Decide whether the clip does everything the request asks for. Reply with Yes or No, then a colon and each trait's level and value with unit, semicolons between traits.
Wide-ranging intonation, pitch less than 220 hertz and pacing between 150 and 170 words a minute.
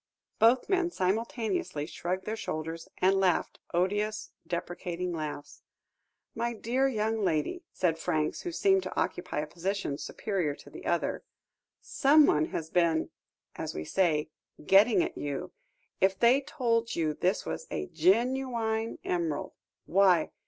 No: wide, 5.7 semitones; high, 190 Hz; slow, 135 wpm